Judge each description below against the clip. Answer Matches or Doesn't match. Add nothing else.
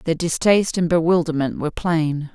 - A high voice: Doesn't match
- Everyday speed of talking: Matches